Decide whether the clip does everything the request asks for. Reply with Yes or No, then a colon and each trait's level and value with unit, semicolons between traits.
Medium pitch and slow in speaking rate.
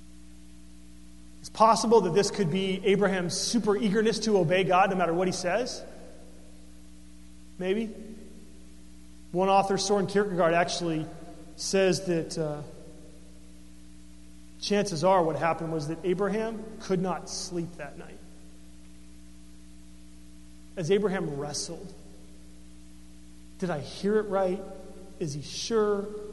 Yes: medium, 165 Hz; slow, 110 wpm